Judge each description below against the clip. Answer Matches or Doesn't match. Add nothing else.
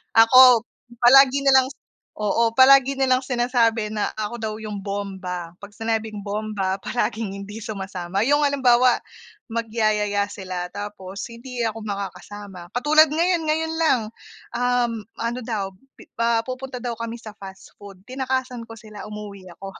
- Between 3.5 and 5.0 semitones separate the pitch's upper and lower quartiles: Matches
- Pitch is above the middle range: Matches